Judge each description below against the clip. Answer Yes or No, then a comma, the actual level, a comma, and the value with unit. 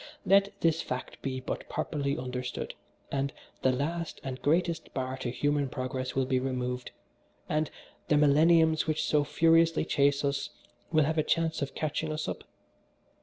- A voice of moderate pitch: Yes, medium, 145 Hz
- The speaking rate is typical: Yes, average, 160 wpm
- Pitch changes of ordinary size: Yes, average, 3.5 semitones